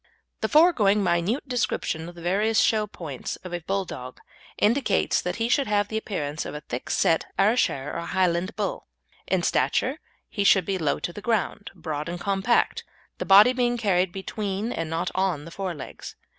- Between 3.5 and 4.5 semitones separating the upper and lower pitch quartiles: Yes, average, 4.0 semitones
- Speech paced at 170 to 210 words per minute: Yes, average, 185 wpm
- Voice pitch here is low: No, high, 195 Hz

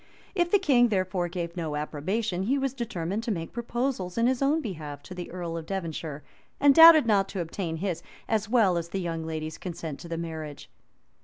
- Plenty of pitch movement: Yes, wide, 6.2 semitones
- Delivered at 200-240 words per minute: Yes, fast, 205 wpm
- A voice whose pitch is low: No, medium, 185 Hz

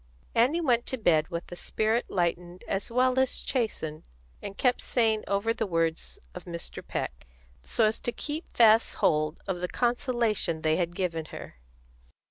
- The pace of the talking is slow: No, average, 165 wpm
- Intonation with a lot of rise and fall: Yes, wide, 6.0 semitones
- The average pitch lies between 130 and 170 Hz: No, high, 205 Hz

